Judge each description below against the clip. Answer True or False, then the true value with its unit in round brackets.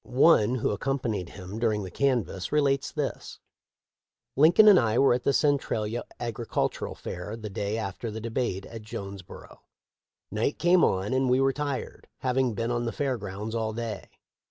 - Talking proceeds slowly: False (170 wpm)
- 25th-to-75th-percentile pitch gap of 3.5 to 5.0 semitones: True (4.3 semitones)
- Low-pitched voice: True (115 Hz)